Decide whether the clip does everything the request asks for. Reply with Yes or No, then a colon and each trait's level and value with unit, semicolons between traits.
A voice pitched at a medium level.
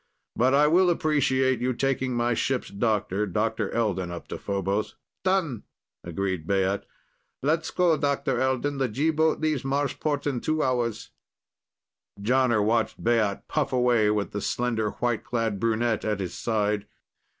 No: low, 120 Hz